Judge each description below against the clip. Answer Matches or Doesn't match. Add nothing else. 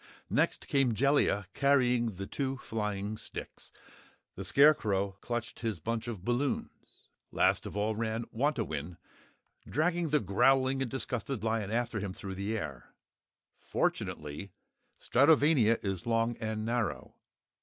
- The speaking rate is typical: Doesn't match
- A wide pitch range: Doesn't match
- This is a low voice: Matches